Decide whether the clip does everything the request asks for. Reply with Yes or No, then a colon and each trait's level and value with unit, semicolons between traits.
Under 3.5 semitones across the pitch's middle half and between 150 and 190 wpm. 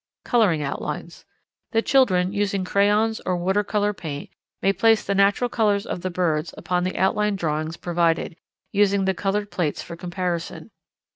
Yes: average, 3.0 semitones; average, 155 wpm